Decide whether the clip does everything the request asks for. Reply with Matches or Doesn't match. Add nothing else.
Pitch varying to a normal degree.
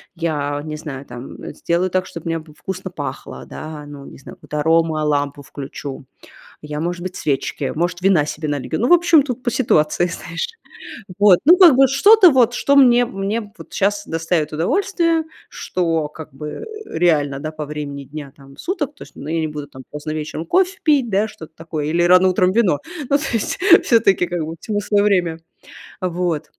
Doesn't match